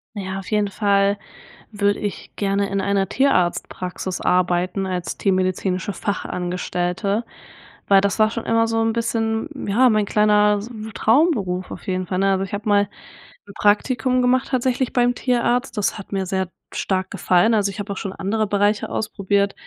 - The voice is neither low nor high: No, high, 200 Hz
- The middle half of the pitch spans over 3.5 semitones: No, average, 2.7 semitones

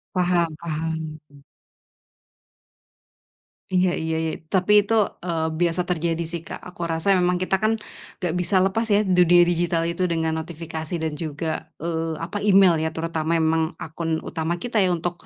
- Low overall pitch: No, medium, 170 Hz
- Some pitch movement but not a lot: No, narrow, 1.8 semitones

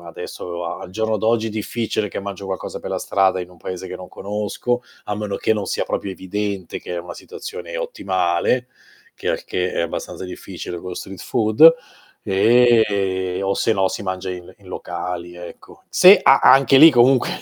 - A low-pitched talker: Yes, low, 100 Hz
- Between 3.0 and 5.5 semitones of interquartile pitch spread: Yes, average, 3.7 semitones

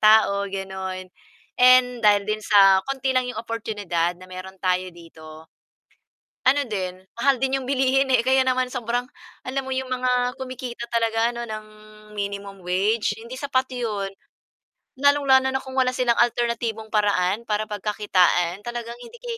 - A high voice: Yes, high, 230 Hz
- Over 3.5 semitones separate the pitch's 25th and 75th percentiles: Yes, average, 4.4 semitones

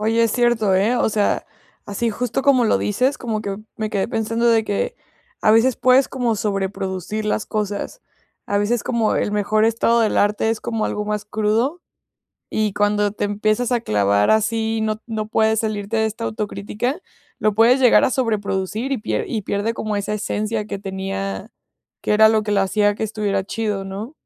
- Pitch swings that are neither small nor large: No, narrow, 1.9 semitones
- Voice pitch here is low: No, high, 215 Hz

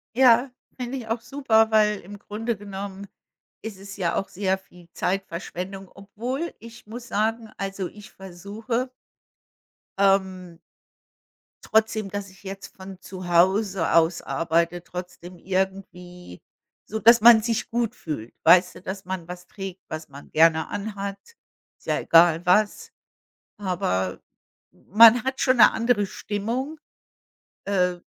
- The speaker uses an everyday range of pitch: Yes, average, 3.6 semitones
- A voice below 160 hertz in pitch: No, high, 195 Hz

